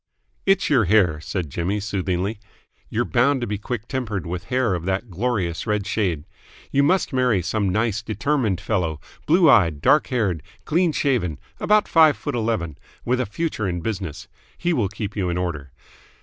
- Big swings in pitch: Yes, wide, 5.8 semitones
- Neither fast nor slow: Yes, average, 175 wpm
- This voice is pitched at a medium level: No, low, 105 Hz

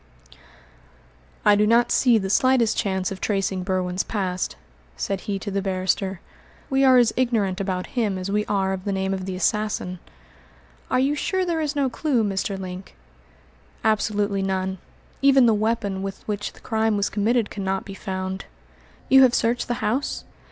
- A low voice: No, high, 205 Hz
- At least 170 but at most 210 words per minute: Yes, average, 175 wpm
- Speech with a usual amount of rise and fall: Yes, average, 3.6 semitones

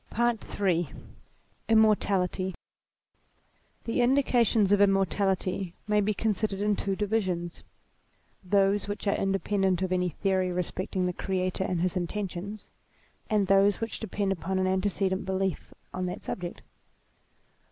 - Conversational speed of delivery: No, slow, 130 wpm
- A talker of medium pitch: No, high, 195 Hz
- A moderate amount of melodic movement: No, narrow, 2.0 semitones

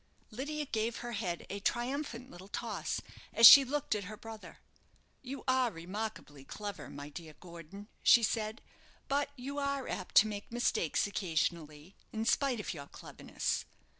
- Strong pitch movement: Yes, wide, 6.1 semitones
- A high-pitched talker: Yes, high, 215 Hz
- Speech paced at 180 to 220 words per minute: No, average, 155 wpm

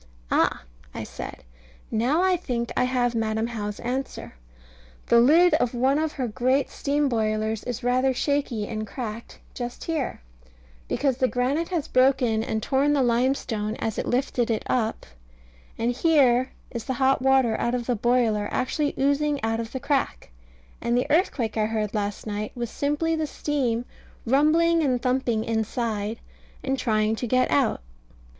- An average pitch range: Yes, average, 3.5 semitones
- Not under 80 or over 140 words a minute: No, average, 165 wpm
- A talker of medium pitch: No, high, 245 Hz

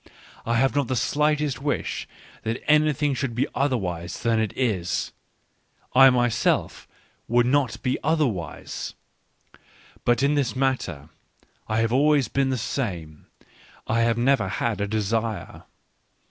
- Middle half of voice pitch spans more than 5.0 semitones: No, average, 3.8 semitones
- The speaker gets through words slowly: Yes, slow, 130 wpm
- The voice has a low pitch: Yes, low, 120 Hz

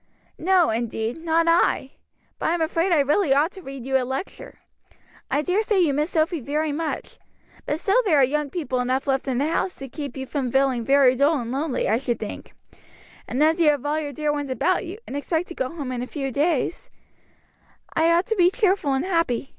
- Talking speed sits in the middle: No, fast, 220 wpm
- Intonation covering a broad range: No, average, 3.9 semitones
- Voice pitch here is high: Yes, very high, 295 Hz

